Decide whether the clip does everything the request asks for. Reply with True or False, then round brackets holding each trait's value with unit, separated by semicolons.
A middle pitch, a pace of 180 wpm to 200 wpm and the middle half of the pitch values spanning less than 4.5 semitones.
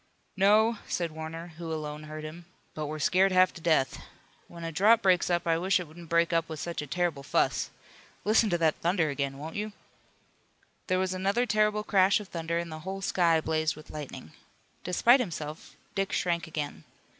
True (170 Hz; 190 wpm; 3.3 semitones)